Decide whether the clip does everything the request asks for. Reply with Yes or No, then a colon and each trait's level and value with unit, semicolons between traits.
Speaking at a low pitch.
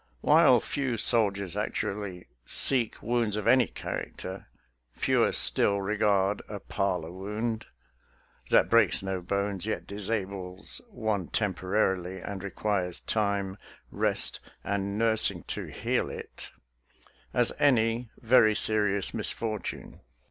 Yes: low, 100 Hz